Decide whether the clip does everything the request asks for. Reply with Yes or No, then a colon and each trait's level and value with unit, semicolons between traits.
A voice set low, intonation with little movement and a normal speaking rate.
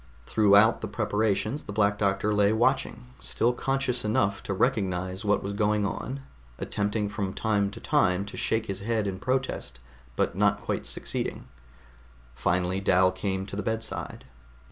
Yes: low, 105 Hz; narrow, 2.2 semitones; average, 155 wpm